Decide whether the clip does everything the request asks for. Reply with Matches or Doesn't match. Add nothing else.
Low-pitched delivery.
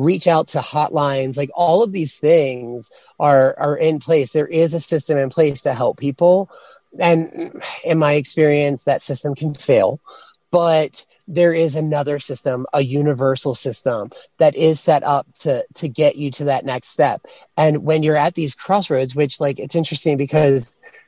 Doesn't match